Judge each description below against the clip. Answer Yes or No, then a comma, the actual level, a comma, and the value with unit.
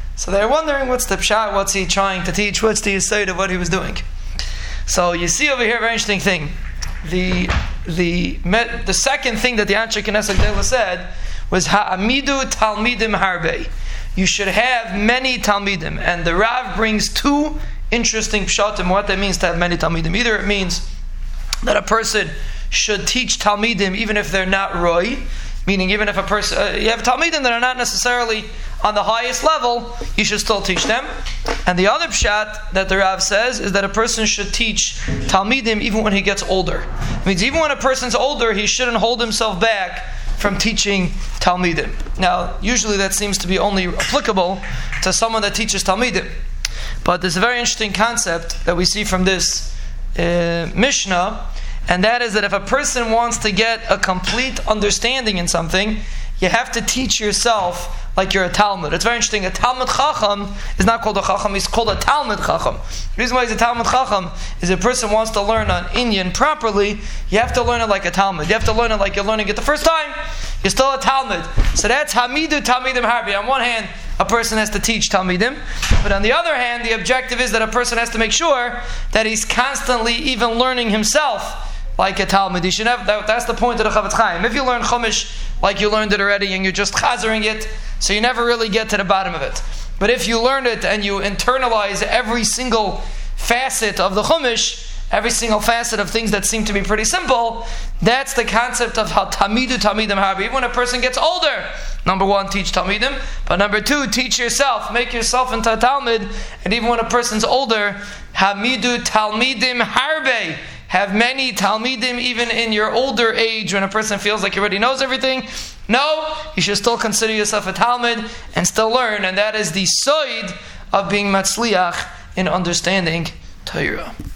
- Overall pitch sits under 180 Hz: No, high, 215 Hz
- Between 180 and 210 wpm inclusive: Yes, average, 200 wpm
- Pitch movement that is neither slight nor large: Yes, average, 3.6 semitones